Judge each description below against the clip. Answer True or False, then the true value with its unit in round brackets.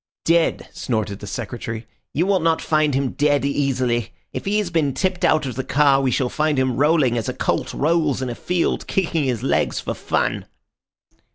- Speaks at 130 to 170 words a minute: False (195 wpm)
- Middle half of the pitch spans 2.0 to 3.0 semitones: False (4.5 semitones)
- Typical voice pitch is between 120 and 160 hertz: True (140 Hz)